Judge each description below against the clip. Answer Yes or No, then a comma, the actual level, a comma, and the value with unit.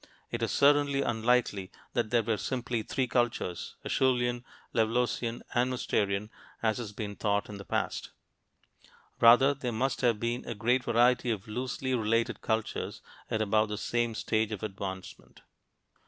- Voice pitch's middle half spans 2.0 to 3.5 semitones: Yes, narrow, 2.4 semitones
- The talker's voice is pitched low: Yes, low, 115 Hz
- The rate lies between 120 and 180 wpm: Yes, average, 150 wpm